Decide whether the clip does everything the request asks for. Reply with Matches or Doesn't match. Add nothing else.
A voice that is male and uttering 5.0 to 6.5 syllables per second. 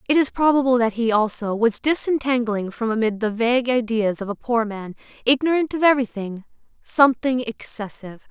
Doesn't match